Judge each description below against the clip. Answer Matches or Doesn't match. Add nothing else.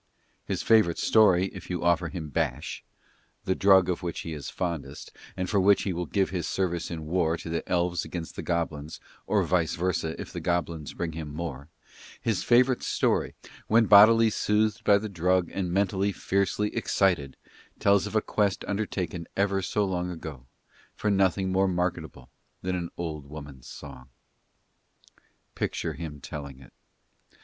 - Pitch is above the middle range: Doesn't match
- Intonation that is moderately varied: Matches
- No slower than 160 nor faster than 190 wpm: Matches